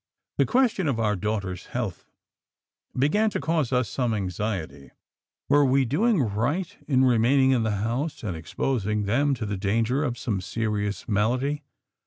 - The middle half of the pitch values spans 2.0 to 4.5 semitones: No, average, 5.0 semitones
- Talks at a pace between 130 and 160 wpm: Yes, average, 155 wpm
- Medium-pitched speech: No, low, 120 Hz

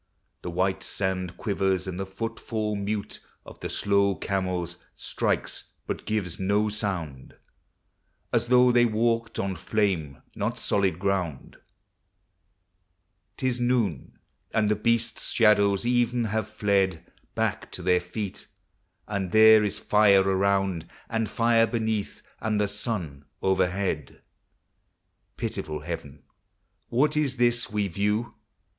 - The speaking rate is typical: No, slow, 125 wpm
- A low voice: Yes, low, 100 Hz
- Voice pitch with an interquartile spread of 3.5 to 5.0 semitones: No, average, 3.1 semitones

